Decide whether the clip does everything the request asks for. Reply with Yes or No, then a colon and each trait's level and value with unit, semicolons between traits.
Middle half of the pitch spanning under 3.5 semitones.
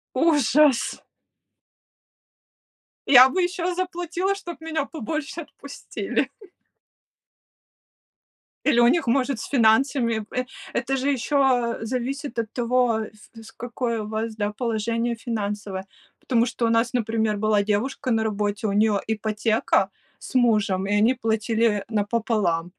No: average, 3.8 semitones